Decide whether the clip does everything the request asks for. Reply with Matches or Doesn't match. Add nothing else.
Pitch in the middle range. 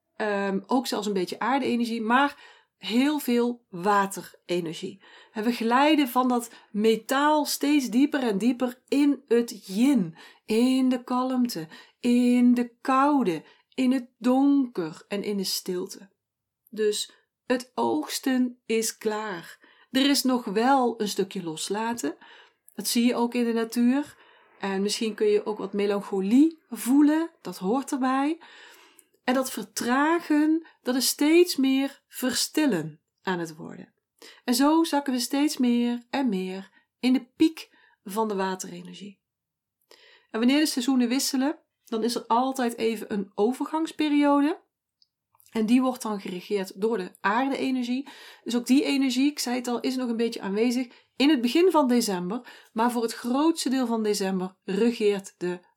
Doesn't match